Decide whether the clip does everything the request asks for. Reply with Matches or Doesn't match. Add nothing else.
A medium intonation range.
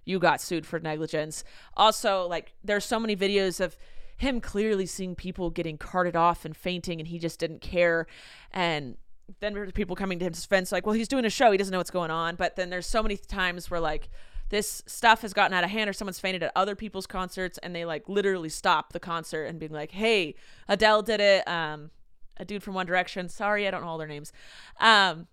Matches